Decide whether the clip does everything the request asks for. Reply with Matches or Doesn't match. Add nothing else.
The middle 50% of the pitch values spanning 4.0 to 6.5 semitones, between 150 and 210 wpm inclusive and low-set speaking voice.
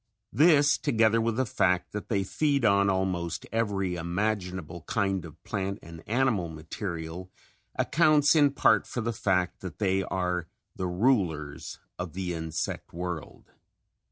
Doesn't match